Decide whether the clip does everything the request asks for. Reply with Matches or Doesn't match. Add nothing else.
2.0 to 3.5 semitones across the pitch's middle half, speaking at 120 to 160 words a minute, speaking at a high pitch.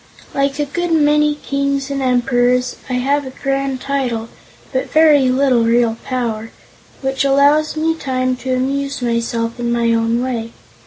Matches